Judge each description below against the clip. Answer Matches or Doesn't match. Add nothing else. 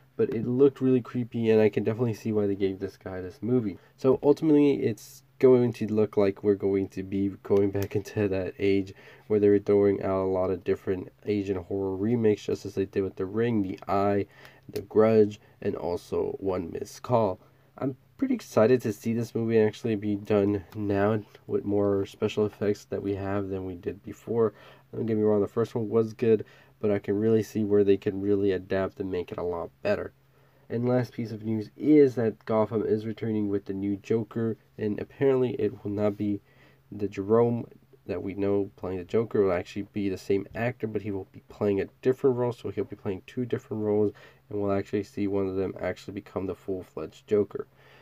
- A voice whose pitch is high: Doesn't match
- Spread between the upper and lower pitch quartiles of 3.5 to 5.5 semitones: Doesn't match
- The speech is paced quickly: Matches